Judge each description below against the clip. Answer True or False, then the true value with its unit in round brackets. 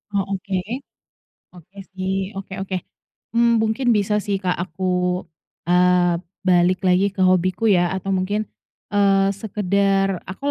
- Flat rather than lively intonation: True (1.6 semitones)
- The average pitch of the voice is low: False (190 Hz)